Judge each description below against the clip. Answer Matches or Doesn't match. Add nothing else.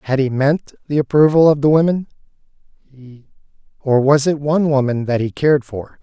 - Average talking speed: Matches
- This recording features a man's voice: Matches